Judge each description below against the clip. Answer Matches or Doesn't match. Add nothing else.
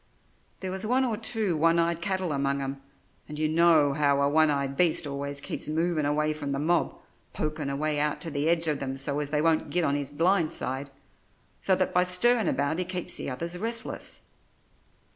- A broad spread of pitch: Doesn't match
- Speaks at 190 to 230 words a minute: Matches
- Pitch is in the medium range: Matches